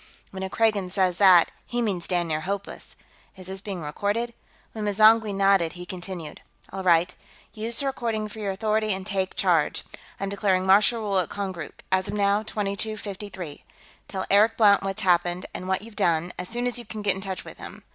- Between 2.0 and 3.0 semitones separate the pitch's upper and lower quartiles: Yes, narrow, 2.5 semitones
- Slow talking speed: No, average, 195 wpm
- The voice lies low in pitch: No, high, 195 Hz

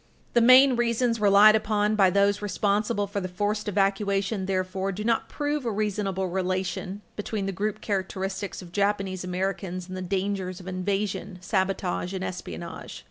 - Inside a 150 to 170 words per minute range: Yes, average, 155 wpm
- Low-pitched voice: No, high, 195 Hz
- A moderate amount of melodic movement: No, narrow, 1.9 semitones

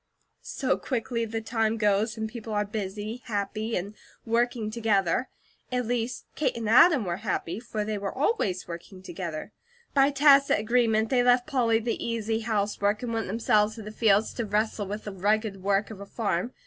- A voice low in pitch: No, high, 220 Hz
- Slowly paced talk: No, average, 180 wpm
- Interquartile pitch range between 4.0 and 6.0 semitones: No, narrow, 2.4 semitones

